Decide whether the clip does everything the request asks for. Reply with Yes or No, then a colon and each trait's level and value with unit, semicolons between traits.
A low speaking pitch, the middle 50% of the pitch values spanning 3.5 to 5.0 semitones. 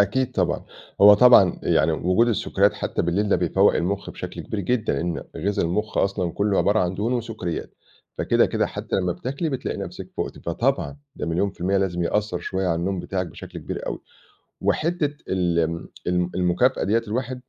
Yes: low, 100 Hz; average, 4.1 semitones